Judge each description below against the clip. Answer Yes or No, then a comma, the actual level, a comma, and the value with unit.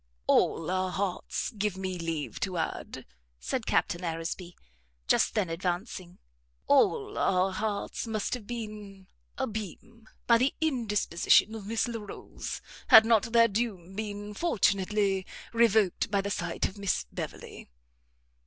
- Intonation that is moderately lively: Yes, average, 3.1 semitones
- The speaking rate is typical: No, slow, 130 wpm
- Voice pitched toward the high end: Yes, high, 205 Hz